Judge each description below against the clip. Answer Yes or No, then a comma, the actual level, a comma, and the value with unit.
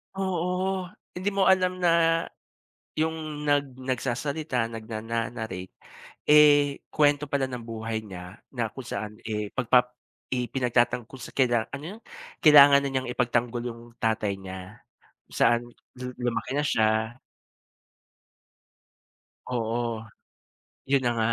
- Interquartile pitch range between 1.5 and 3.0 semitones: No, average, 4.2 semitones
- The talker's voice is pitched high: No, low, 125 Hz